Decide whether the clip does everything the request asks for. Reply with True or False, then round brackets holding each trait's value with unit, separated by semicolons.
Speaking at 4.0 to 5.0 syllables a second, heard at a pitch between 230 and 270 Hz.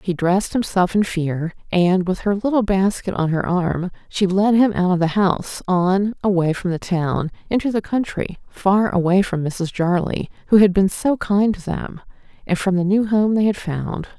False (4.6 syllables/s; 190 Hz)